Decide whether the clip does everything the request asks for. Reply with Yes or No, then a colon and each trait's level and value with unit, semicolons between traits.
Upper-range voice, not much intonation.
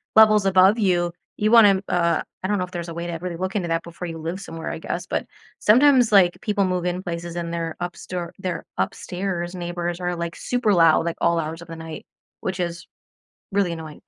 No: medium, 175 Hz; narrow, 2.2 semitones